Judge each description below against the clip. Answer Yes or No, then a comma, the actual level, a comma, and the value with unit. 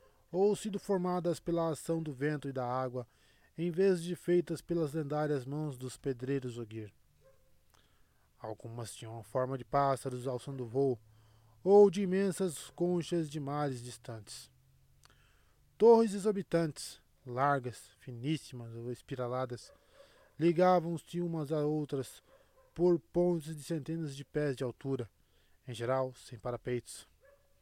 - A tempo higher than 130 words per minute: No, average, 125 wpm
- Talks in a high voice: No, medium, 140 Hz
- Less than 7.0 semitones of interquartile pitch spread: Yes, wide, 5.5 semitones